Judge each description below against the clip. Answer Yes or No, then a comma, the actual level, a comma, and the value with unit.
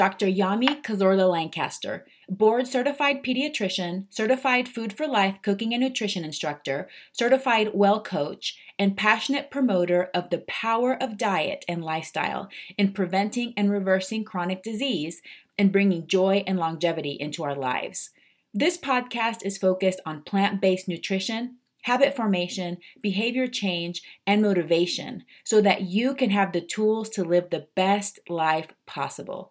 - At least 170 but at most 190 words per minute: No, average, 140 wpm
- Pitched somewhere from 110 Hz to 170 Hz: No, high, 200 Hz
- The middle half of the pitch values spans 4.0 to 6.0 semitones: Yes, average, 4.5 semitones